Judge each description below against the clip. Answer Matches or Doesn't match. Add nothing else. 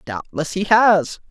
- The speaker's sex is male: Matches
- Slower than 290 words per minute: Matches